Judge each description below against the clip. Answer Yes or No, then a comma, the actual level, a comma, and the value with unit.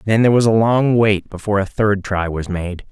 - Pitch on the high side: No, low, 105 Hz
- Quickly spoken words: Yes, fast, 245 wpm